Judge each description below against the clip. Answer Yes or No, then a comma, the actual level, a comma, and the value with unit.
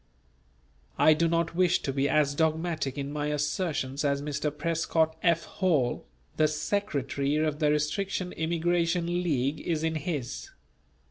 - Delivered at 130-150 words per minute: Yes, average, 140 wpm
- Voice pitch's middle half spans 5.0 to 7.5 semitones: No, average, 2.7 semitones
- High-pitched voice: No, medium, 155 Hz